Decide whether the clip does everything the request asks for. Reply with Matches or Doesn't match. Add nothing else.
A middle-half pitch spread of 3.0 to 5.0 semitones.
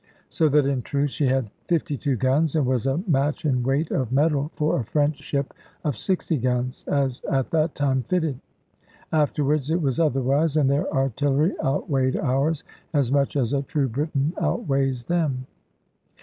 Doesn't match